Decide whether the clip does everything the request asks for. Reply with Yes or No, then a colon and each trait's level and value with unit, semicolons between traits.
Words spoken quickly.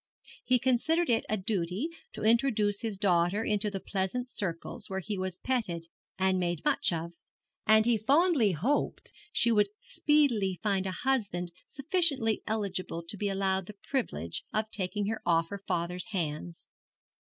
No: average, 155 wpm